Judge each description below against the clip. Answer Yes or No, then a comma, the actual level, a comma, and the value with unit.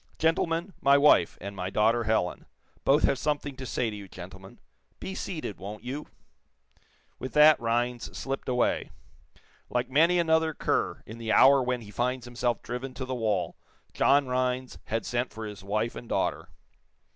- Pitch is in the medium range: No, low, 125 Hz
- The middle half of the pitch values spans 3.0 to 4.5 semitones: Yes, average, 4.1 semitones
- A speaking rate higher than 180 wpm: No, average, 170 wpm